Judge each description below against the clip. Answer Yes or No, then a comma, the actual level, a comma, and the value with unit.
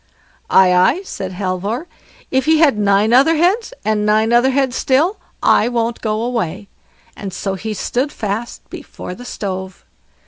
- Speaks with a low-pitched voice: No, high, 225 Hz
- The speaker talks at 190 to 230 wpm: No, average, 160 wpm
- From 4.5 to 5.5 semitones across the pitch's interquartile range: Yes, average, 4.9 semitones